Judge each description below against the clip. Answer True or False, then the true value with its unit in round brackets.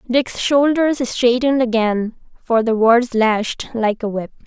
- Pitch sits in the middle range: False (240 Hz)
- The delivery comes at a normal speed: True (150 wpm)